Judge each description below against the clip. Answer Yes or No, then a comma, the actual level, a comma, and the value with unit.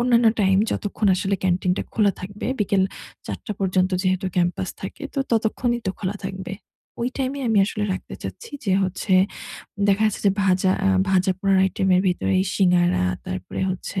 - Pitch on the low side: No, high, 190 Hz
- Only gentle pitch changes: Yes, narrow, 2.1 semitones